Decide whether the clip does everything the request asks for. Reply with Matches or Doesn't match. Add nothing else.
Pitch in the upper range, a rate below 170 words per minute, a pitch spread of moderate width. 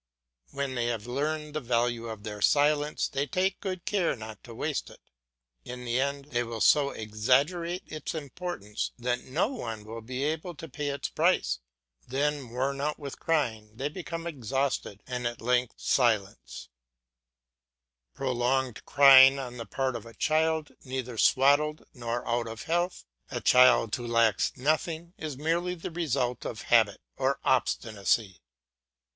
Doesn't match